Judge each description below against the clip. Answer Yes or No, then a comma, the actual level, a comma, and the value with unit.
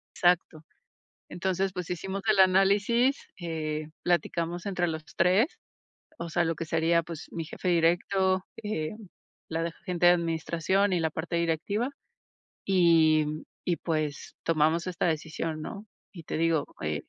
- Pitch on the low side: No, medium, 170 Hz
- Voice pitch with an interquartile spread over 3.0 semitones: No, narrow, 2.6 semitones